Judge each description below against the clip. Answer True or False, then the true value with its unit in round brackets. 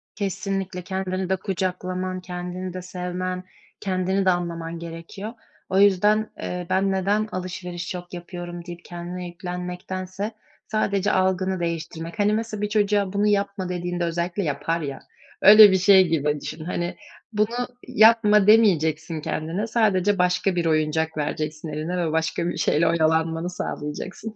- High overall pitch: False (180 Hz)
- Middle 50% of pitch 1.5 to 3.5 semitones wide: True (2.5 semitones)